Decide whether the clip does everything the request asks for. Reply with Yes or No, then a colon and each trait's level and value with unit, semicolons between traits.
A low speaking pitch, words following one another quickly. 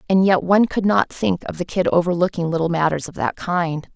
No: medium, 175 Hz; fast, 230 wpm